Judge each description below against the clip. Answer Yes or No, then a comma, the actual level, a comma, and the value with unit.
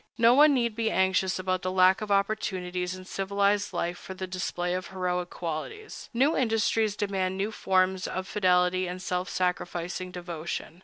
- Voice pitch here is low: No, medium, 185 Hz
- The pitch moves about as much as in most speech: No, narrow, 2.3 semitones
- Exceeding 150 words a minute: Yes, average, 165 wpm